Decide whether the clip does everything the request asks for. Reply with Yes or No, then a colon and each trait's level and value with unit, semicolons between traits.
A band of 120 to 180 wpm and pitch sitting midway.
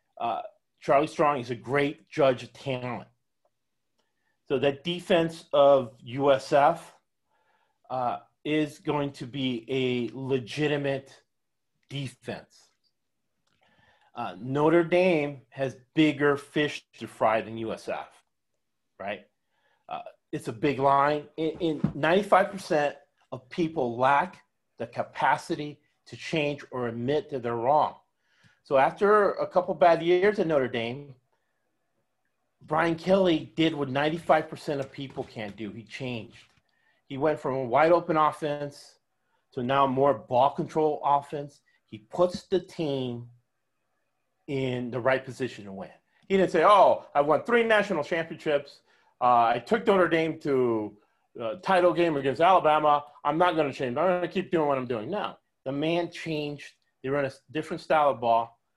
Yes: average, 145 wpm; medium, 145 Hz